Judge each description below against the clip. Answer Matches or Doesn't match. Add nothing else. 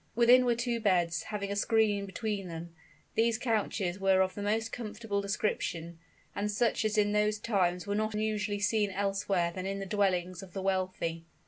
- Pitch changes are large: Doesn't match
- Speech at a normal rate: Matches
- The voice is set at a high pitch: Matches